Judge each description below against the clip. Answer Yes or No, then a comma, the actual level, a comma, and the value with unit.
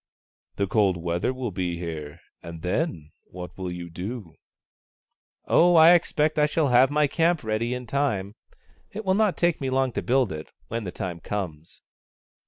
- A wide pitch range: Yes, wide, 8.8 semitones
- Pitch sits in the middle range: No, low, 110 Hz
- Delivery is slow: No, average, 190 wpm